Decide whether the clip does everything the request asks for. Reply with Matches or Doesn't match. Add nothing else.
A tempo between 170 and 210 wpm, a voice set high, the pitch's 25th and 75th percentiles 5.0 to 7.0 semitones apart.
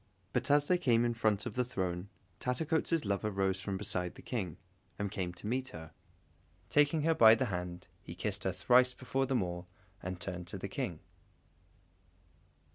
Doesn't match